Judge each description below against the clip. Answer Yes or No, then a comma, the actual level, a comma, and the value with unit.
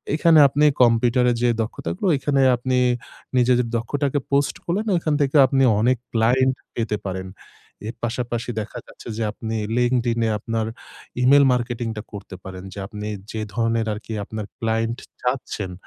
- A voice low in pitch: Yes, low, 120 Hz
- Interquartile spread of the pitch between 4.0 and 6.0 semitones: No, narrow, 2.6 semitones